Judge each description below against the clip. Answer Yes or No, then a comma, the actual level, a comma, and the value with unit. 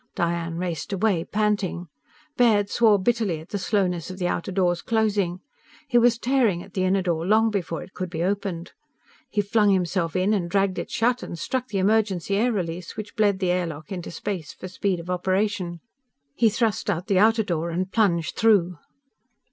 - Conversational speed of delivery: Yes, average, 190 wpm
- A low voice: No, high, 190 Hz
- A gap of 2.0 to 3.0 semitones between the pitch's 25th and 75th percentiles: No, average, 3.4 semitones